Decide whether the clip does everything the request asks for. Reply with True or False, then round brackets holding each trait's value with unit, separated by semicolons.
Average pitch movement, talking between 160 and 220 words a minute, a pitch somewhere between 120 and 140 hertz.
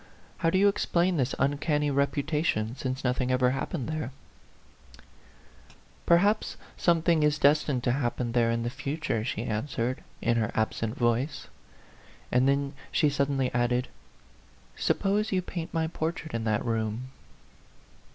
False (4.7 semitones; 145 wpm; 135 Hz)